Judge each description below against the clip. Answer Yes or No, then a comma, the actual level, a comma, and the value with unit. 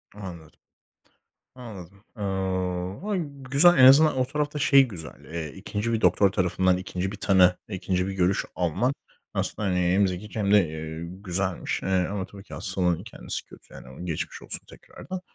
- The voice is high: No, very low, 95 Hz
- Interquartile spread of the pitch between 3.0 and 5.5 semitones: Yes, average, 3.4 semitones